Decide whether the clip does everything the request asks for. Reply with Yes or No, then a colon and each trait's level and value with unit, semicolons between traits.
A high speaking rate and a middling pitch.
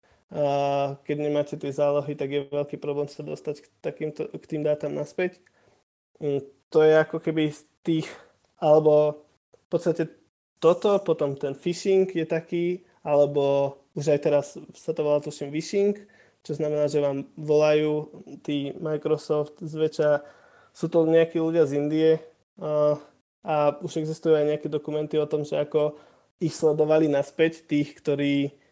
No: average, 140 wpm; medium, 150 Hz